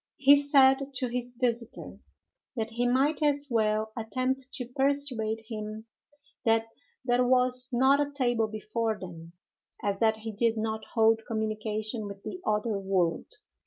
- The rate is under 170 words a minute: Yes, average, 145 wpm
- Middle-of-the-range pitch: No, high, 230 Hz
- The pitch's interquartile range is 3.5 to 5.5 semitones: No, average, 3.0 semitones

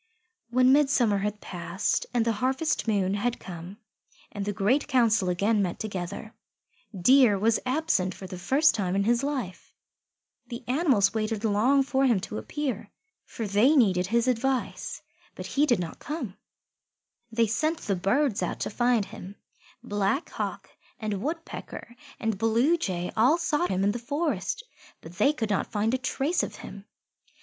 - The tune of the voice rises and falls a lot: No, average, 4.9 semitones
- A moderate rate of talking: Yes, average, 160 wpm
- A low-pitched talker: No, high, 225 Hz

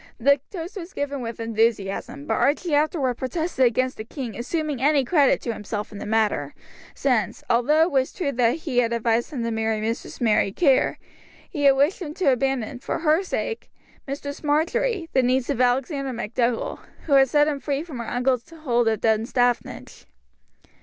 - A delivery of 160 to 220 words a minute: Yes, average, 180 wpm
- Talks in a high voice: Yes, very high, 260 Hz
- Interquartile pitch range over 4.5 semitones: No, average, 4.1 semitones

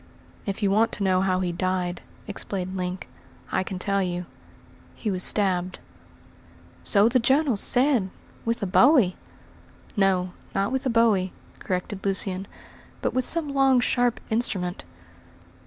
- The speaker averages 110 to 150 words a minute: Yes, average, 140 wpm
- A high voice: Yes, high, 195 Hz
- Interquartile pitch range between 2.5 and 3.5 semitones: No, average, 4.1 semitones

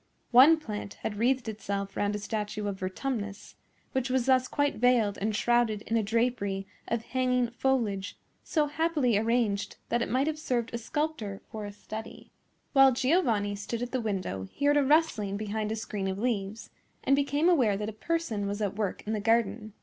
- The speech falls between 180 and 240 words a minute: Yes, average, 190 wpm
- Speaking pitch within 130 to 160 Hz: No, high, 225 Hz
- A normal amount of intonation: Yes, average, 4.1 semitones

